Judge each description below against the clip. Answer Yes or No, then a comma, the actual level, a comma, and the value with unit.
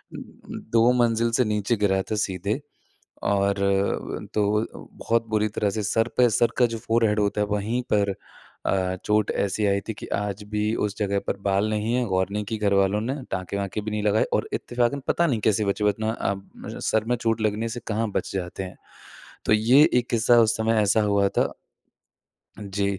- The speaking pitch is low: Yes, low, 105 Hz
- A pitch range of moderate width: No, narrow, 2.1 semitones